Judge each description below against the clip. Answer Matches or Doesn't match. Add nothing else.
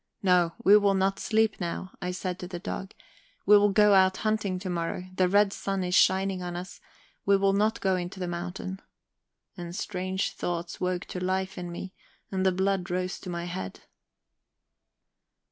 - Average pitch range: Doesn't match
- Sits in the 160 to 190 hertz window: Matches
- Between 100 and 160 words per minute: Doesn't match